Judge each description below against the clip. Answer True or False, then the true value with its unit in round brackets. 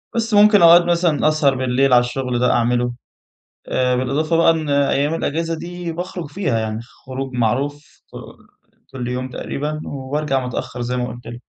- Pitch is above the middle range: False (135 Hz)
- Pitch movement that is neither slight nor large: True (4.7 semitones)